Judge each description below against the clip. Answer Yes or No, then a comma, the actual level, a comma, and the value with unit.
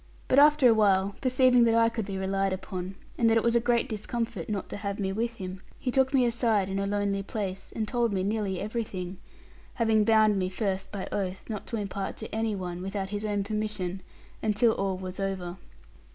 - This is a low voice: No, high, 205 Hz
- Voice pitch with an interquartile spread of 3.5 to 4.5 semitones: No, average, 3.0 semitones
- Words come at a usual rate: No, fast, 210 wpm